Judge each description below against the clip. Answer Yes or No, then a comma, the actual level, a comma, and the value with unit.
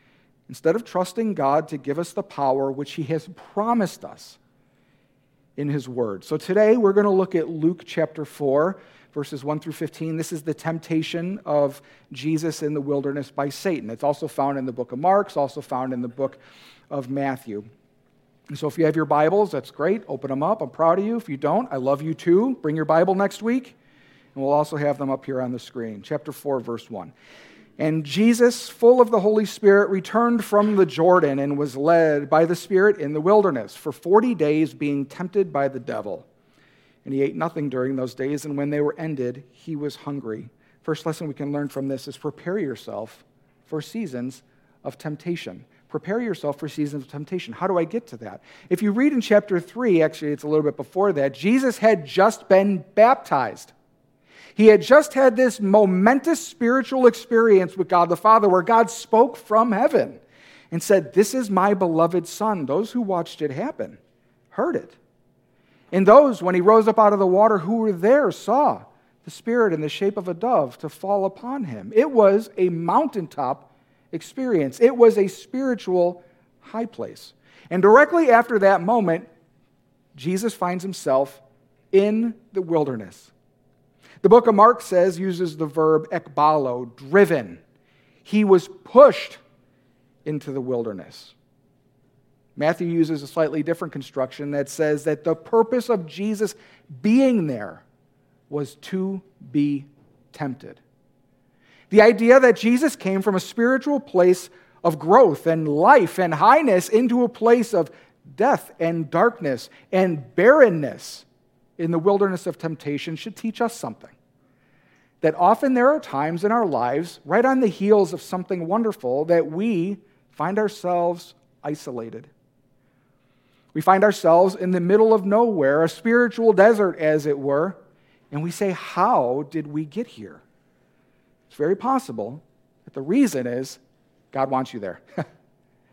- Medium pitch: Yes, medium, 165 Hz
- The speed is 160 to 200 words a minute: Yes, average, 170 wpm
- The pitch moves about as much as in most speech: No, wide, 6.5 semitones